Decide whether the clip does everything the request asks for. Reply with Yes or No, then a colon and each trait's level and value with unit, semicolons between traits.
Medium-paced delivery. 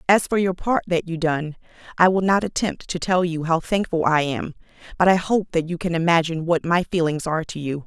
No: fast, 235 wpm